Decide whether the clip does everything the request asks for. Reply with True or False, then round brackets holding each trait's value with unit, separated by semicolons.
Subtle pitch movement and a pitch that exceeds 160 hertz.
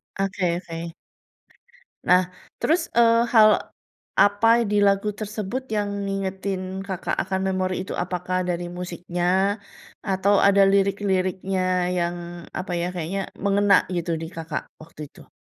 True (2.1 semitones; 190 Hz)